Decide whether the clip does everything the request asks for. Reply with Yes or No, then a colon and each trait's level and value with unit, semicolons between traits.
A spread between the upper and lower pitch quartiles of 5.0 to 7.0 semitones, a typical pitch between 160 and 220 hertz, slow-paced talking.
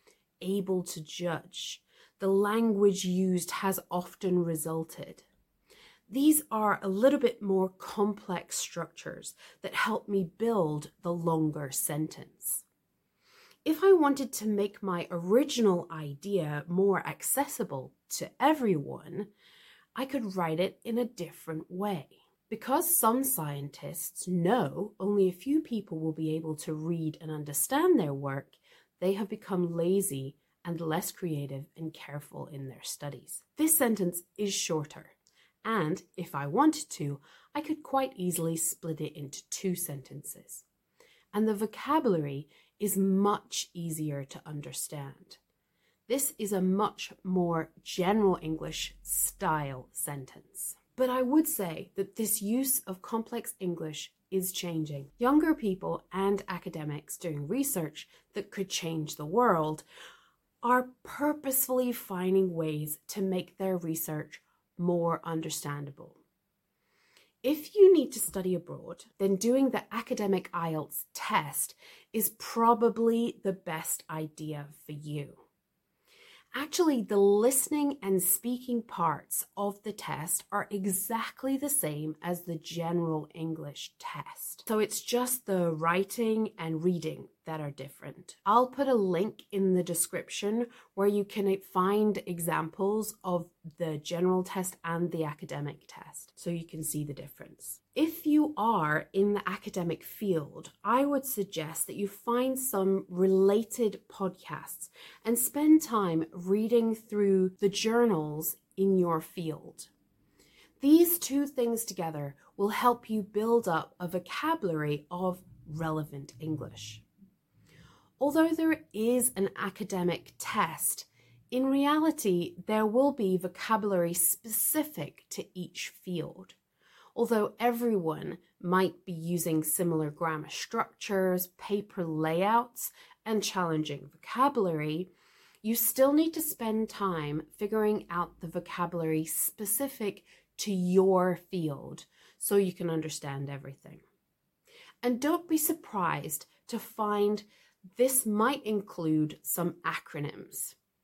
Yes: wide, 5.5 semitones; high, 190 Hz; slow, 125 wpm